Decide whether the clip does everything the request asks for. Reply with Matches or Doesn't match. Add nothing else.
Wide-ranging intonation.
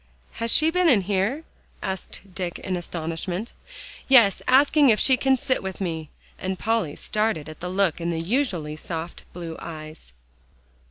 Matches